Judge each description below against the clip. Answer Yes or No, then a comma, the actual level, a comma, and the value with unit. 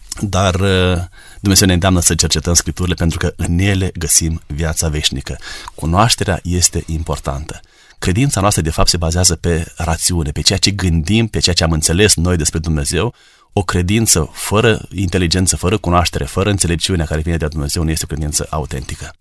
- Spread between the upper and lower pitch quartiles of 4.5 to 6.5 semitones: No, narrow, 2.6 semitones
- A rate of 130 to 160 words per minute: No, fast, 170 wpm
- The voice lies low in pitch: Yes, very low, 85 Hz